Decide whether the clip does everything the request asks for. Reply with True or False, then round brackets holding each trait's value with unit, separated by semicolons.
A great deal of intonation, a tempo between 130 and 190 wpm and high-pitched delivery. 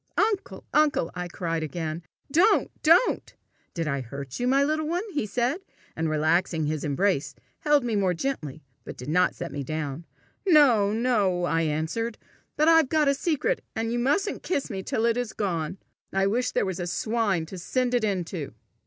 True (8.7 semitones; 185 wpm; 200 Hz)